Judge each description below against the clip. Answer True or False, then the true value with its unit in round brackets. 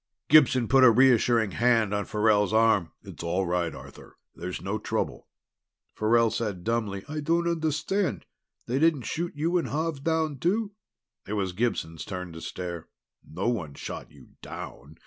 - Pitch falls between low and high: False (115 Hz)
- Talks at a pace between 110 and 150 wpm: False (160 wpm)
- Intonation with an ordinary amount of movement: False (7.5 semitones)